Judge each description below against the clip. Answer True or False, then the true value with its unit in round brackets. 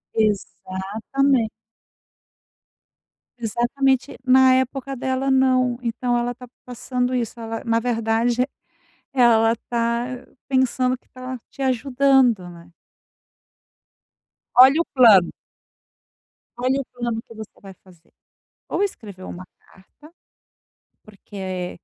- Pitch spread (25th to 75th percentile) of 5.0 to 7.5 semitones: False (2.8 semitones)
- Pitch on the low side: False (240 Hz)